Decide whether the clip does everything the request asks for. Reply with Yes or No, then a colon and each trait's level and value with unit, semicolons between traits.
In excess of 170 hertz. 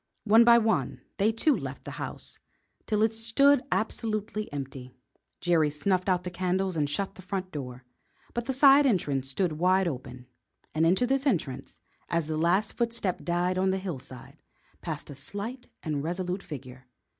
Yes: medium, 185 Hz